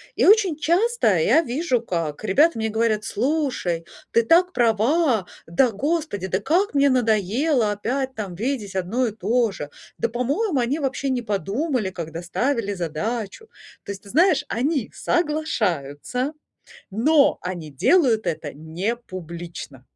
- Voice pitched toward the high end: Yes, high, 230 Hz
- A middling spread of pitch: No, wide, 7.1 semitones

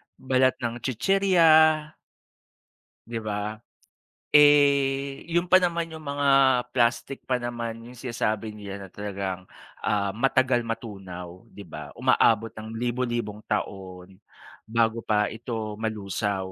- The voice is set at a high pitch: No, low, 115 Hz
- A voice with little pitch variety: No, average, 4.2 semitones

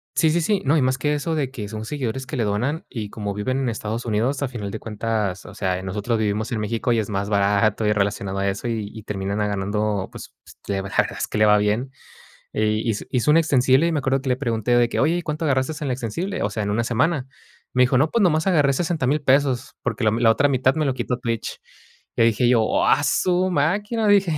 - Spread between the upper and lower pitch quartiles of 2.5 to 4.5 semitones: No, average, 5.3 semitones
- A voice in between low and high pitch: No, low, 120 Hz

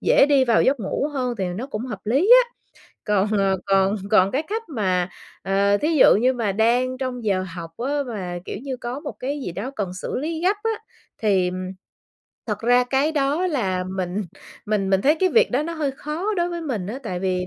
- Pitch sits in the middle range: No, high, 240 Hz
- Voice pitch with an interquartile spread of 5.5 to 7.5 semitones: Yes, wide, 6.5 semitones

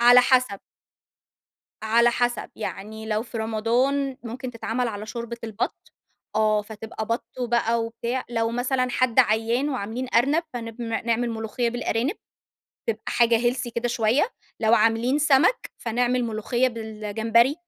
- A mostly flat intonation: Yes, narrow, 2.0 semitones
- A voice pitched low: No, high, 235 Hz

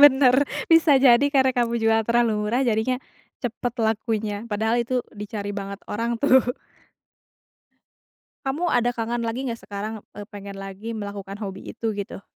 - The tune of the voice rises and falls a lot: No, average, 2.9 semitones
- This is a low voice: No, high, 225 Hz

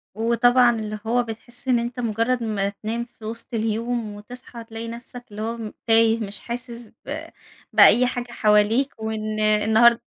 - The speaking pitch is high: Yes, high, 230 Hz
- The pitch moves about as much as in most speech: No, narrow, 1.8 semitones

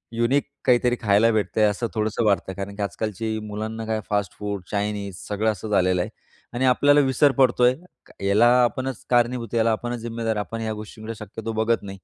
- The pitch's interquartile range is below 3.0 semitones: Yes, narrow, 2.5 semitones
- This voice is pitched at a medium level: No, low, 110 Hz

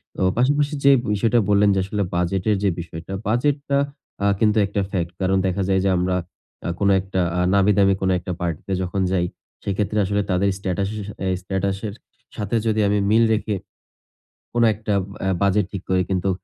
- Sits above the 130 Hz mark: No, low, 100 Hz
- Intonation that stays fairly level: Yes, narrow, 2.1 semitones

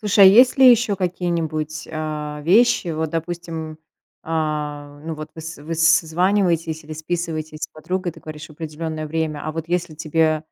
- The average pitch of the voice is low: No, medium, 160 Hz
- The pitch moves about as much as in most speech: No, narrow, 2.0 semitones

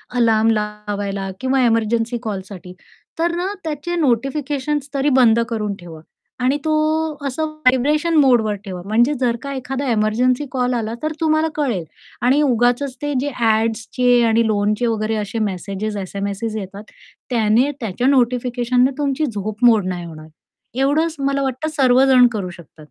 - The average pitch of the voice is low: No, high, 240 Hz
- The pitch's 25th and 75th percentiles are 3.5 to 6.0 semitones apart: Yes, average, 4.4 semitones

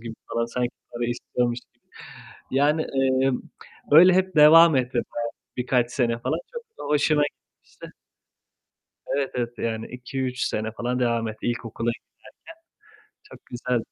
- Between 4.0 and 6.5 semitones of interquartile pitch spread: No, average, 3.0 semitones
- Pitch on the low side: Yes, low, 125 Hz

